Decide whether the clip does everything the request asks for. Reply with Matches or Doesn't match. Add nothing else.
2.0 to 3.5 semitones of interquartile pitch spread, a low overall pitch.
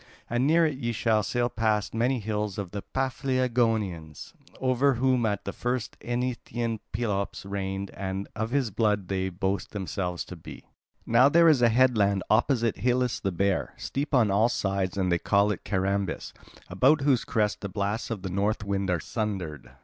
Doesn't match